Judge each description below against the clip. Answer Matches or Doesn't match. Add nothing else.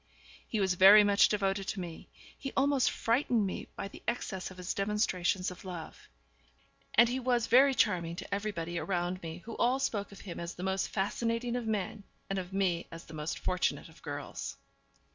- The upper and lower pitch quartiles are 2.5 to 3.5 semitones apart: Doesn't match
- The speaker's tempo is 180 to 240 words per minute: Matches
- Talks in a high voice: Matches